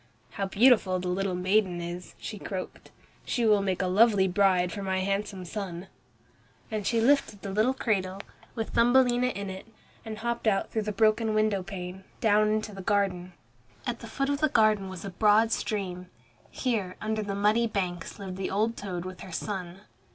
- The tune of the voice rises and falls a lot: No, average, 2.7 semitones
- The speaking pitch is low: No, high, 200 Hz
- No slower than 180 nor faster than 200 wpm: Yes, average, 185 wpm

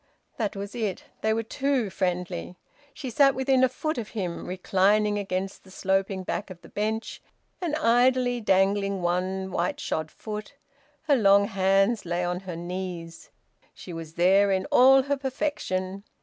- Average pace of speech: Yes, average, 160 wpm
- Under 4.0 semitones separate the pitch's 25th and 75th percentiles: No, average, 4.4 semitones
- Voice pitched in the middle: No, high, 195 Hz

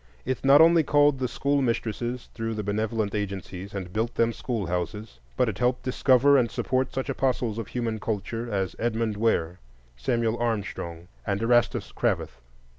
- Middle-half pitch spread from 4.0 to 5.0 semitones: No, average, 3.5 semitones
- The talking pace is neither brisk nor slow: Yes, average, 160 wpm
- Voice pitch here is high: No, low, 115 Hz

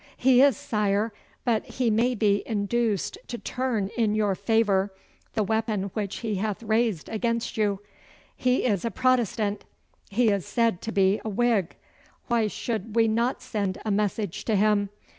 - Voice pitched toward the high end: Yes, high, 215 Hz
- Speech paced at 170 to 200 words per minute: No, average, 160 wpm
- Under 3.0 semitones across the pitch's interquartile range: Yes, narrow, 2.4 semitones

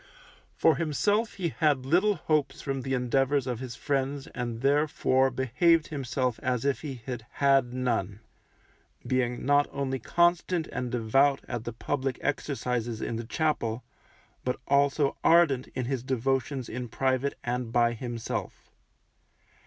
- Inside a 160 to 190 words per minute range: No, average, 140 wpm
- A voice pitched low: Yes, low, 130 Hz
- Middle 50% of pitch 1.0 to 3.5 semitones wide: Yes, average, 2.8 semitones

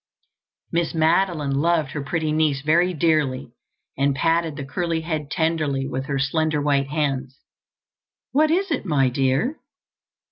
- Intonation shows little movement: No, average, 3.3 semitones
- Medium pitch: Yes, medium, 155 Hz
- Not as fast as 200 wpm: Yes, average, 140 wpm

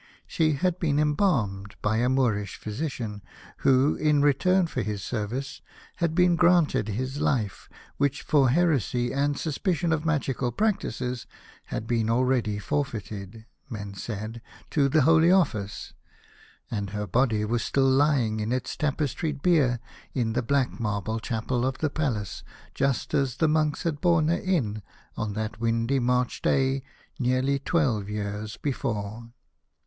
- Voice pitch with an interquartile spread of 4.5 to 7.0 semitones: Yes, average, 5.3 semitones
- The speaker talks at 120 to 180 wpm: Yes, average, 145 wpm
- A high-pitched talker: No, low, 130 Hz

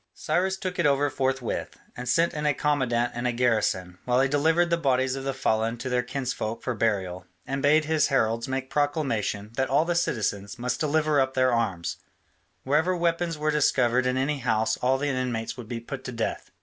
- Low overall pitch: Yes, low, 130 Hz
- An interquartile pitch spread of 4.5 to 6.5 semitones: No, average, 3.9 semitones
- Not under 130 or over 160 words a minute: No, average, 200 wpm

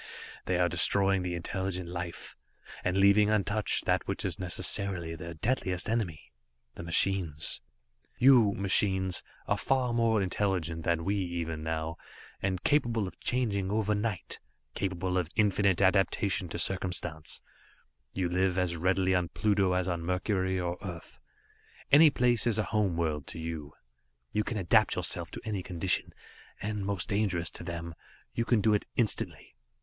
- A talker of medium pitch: No, very low, 95 Hz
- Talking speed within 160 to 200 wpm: No, average, 150 wpm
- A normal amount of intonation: Yes, average, 3.2 semitones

